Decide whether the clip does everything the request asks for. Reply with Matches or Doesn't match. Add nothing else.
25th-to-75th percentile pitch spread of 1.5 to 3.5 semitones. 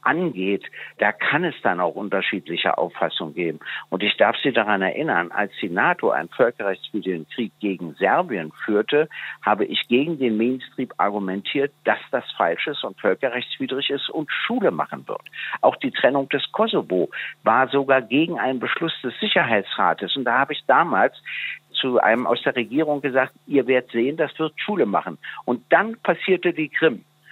Doesn't match